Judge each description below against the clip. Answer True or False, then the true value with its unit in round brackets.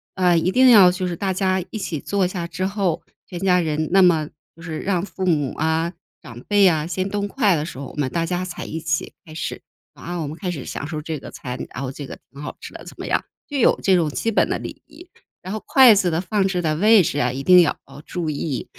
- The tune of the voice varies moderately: True (3.6 semitones)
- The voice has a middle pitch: True (175 Hz)